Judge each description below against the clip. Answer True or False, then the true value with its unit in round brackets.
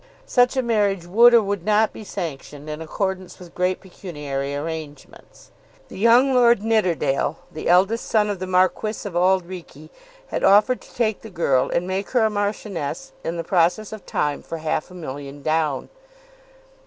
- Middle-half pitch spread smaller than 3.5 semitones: False (5.1 semitones)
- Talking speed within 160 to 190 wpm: True (170 wpm)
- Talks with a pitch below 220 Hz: True (185 Hz)